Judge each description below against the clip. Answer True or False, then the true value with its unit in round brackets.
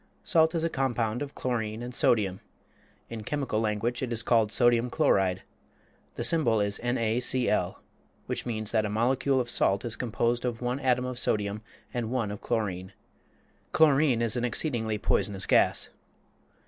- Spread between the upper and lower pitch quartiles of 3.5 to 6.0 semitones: False (2.8 semitones)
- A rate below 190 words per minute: True (160 wpm)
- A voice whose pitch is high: False (120 Hz)